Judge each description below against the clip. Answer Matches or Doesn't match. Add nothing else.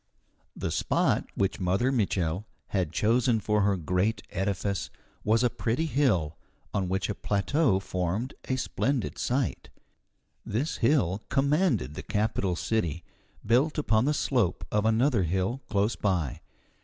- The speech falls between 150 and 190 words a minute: Doesn't match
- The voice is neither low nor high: Doesn't match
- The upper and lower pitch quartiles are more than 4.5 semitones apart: Matches